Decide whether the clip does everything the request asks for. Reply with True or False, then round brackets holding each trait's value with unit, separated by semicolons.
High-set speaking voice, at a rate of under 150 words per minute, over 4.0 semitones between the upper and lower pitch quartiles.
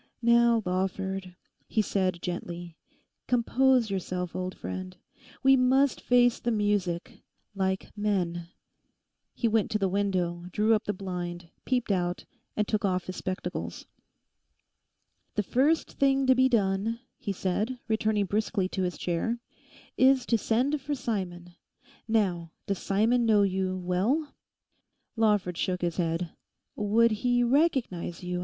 True (200 Hz; 135 wpm; 4.5 semitones)